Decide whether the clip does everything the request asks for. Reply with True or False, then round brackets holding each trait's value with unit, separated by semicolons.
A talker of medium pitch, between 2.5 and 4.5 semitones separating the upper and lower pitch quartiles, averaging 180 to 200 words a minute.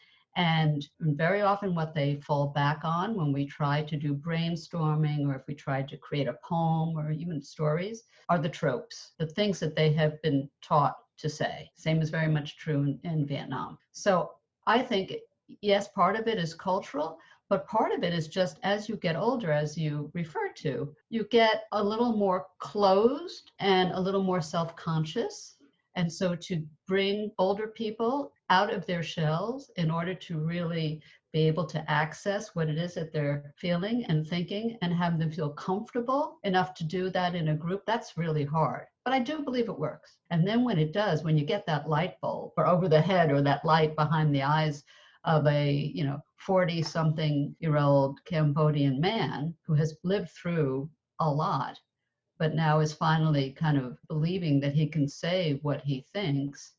True (160 Hz; 4.0 semitones; 190 wpm)